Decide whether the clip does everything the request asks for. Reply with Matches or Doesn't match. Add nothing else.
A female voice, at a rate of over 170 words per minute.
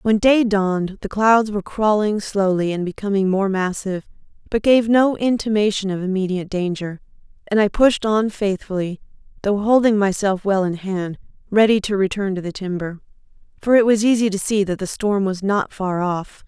Matches